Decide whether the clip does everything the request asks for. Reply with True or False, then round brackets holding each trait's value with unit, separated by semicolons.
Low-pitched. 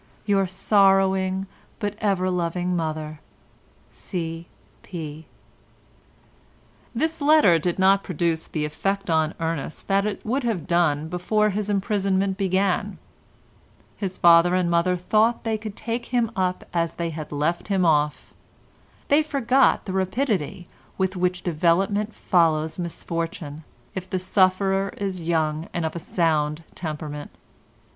False (185 Hz)